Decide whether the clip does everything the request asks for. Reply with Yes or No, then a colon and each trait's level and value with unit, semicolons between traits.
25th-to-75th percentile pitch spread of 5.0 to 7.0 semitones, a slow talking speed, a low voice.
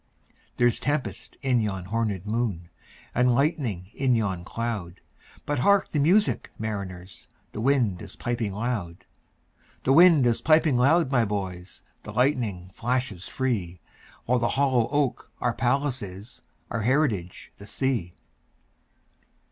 Yes: average, 5.3 semitones; slow, 110 wpm; low, 120 Hz